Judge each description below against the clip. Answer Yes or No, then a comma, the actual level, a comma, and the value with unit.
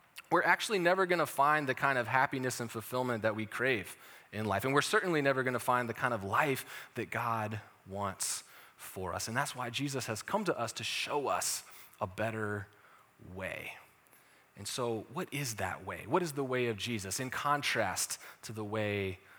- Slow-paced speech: No, average, 200 wpm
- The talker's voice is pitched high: No, low, 120 Hz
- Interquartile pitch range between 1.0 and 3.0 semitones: No, average, 4.5 semitones